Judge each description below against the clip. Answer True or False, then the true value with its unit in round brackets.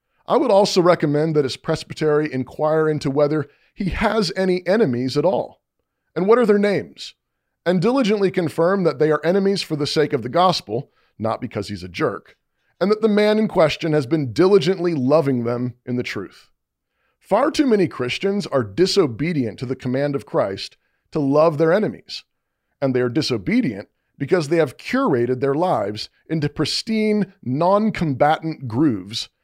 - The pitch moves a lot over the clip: True (5.7 semitones)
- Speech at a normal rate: True (170 wpm)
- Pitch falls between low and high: True (155 Hz)